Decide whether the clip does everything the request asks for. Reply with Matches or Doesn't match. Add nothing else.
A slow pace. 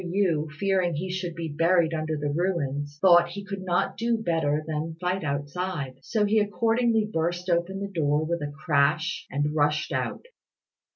Doesn't match